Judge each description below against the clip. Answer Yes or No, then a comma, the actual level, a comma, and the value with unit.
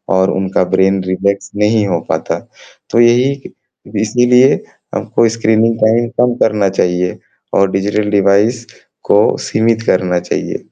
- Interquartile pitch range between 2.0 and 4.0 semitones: Yes, average, 3.1 semitones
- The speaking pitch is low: Yes, low, 105 Hz